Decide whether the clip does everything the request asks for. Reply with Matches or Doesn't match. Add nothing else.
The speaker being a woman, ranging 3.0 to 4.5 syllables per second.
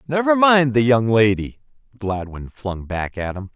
Doesn't match